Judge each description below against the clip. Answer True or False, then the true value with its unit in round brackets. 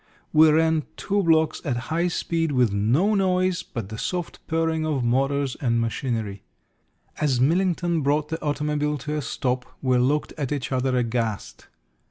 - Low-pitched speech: False (145 Hz)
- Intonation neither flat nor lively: True (4.5 semitones)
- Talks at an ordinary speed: True (160 wpm)